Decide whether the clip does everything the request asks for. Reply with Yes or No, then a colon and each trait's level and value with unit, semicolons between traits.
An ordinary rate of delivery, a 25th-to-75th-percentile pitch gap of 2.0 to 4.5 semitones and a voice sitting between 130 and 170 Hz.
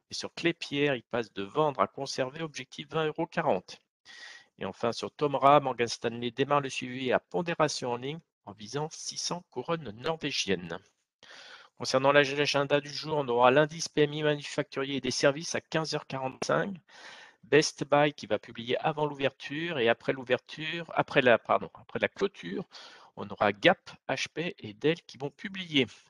Yes: average, 160 wpm; average, 3.6 semitones; medium, 140 Hz